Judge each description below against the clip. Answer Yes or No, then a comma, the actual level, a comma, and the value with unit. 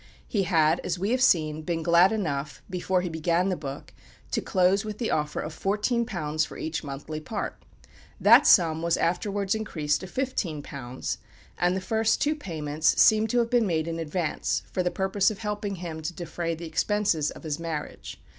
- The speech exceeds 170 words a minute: Yes, average, 185 wpm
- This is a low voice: No, medium, 175 Hz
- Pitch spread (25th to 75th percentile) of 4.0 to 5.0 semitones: Yes, average, 4.6 semitones